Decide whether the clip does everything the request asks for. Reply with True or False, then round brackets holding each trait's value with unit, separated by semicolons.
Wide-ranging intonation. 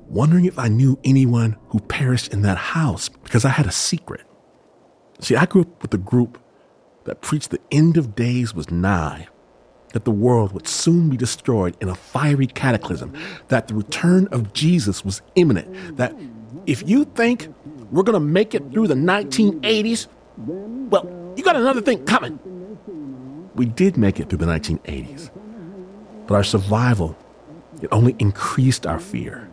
True (8.9 semitones)